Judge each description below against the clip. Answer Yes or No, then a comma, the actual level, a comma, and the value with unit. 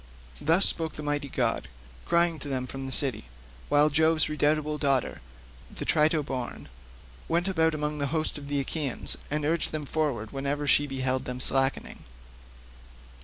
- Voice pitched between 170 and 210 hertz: No, medium, 145 Hz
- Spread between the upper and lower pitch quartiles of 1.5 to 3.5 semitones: Yes, narrow, 2.5 semitones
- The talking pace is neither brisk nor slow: Yes, average, 160 wpm